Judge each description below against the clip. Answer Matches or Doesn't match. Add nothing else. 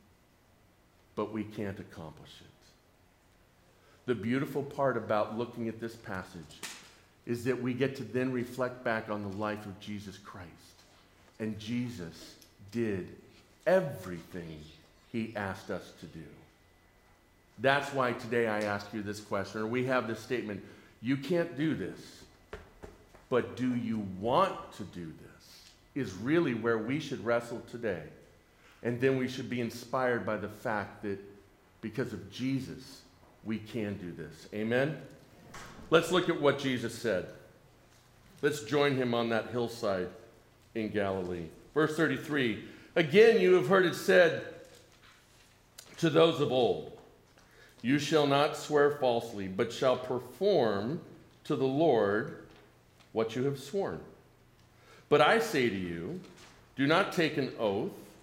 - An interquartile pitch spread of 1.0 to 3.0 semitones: Doesn't match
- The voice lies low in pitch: Matches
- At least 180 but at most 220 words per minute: Doesn't match